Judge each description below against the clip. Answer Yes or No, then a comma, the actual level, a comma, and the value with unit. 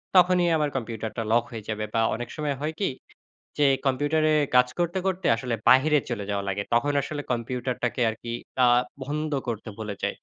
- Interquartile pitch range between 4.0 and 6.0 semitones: Yes, average, 4.9 semitones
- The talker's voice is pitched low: Yes, low, 130 Hz